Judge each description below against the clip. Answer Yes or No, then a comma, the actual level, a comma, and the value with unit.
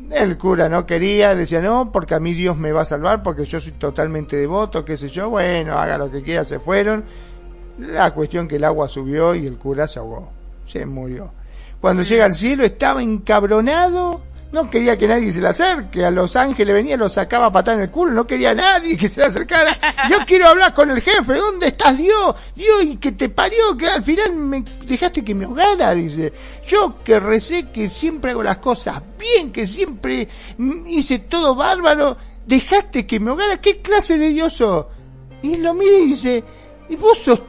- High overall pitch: Yes, high, 230 Hz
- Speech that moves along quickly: Yes, fast, 205 wpm